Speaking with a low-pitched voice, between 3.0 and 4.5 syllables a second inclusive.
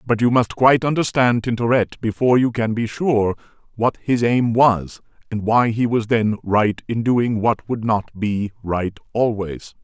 Yes: low, 115 Hz; 4.3 syllables/s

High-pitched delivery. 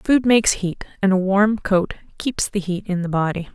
Yes: high, 195 Hz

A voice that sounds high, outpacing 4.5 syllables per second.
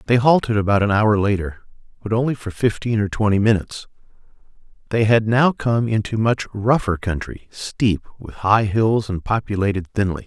No: low, 105 Hz; 5.1 syllables/s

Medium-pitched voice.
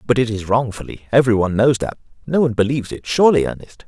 No: low, 120 Hz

